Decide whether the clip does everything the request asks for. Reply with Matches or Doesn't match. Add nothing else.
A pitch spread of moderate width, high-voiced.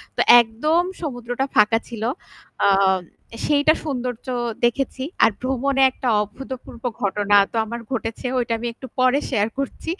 Matches